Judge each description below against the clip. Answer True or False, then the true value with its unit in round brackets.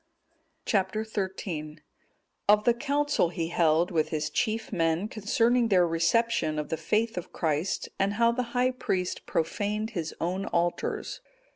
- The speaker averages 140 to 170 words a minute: True (145 wpm)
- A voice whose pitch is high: True (195 Hz)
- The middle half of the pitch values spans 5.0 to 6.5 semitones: True (5.6 semitones)